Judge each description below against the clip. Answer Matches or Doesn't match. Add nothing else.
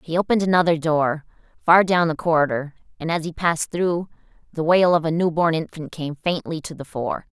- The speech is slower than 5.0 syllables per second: Doesn't match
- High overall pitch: Doesn't match